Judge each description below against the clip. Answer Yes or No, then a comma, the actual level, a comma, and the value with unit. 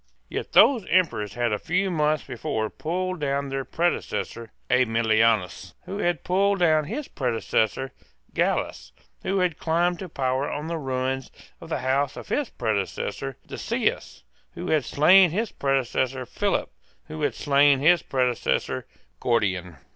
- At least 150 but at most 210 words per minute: No, average, 140 wpm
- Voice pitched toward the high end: No, medium, 140 Hz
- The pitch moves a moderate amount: No, wide, 6.4 semitones